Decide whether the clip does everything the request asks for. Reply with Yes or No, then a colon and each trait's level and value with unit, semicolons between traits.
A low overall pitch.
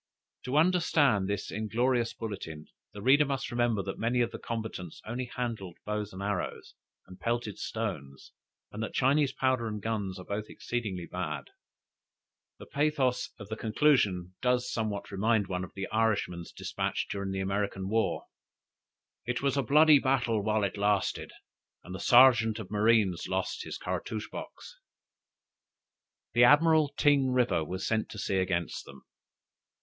Yes: low, 110 Hz